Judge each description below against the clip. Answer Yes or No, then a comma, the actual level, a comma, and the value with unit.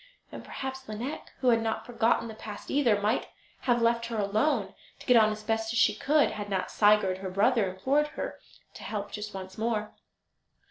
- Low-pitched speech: No, high, 220 Hz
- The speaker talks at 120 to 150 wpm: No, average, 190 wpm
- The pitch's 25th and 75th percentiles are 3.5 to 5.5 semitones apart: No, narrow, 2.6 semitones